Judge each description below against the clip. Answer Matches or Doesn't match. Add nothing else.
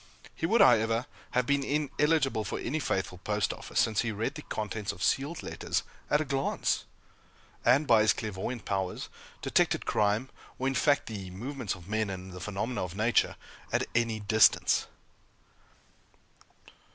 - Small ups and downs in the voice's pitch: Doesn't match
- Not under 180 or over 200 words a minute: Doesn't match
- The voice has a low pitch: Matches